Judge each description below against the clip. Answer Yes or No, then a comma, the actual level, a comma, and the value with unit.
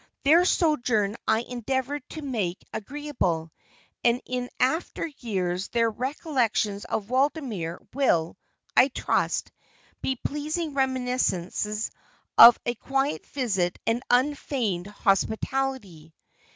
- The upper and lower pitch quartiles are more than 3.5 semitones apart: Yes, average, 5.1 semitones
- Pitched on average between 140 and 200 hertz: No, high, 245 Hz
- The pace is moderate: No, slow, 100 wpm